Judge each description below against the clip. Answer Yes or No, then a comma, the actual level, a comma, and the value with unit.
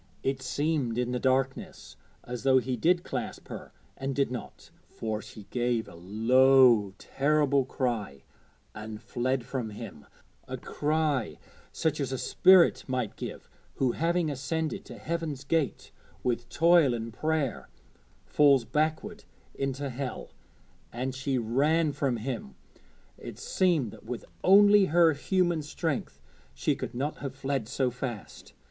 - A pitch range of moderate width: Yes, average, 4.1 semitones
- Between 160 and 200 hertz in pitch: No, low, 135 Hz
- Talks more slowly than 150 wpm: Yes, average, 140 wpm